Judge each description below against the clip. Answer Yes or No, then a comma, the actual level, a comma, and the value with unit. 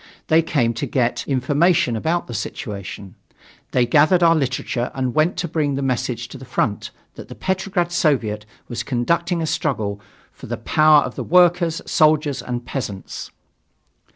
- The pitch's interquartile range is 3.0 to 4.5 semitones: No, wide, 5.4 semitones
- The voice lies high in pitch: No, medium, 140 Hz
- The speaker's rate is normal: Yes, average, 160 wpm